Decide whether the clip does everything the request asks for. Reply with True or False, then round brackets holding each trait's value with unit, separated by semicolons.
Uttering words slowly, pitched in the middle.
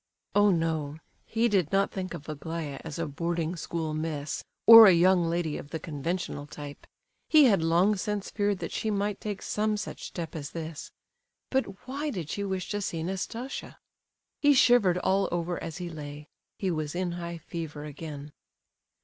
False (175 wpm; 170 Hz)